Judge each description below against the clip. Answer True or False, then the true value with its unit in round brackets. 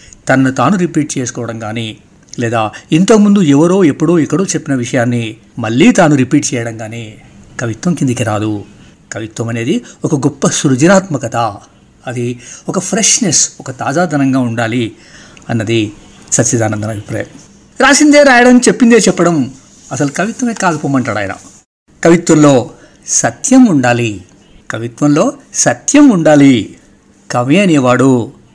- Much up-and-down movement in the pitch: True (6.8 semitones)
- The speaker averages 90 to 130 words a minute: True (105 wpm)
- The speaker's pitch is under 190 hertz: True (135 Hz)